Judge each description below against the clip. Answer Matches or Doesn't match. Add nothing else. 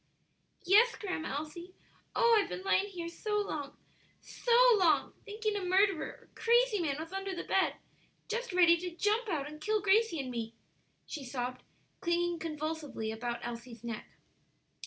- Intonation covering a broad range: Matches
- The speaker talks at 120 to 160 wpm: Matches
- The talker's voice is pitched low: Doesn't match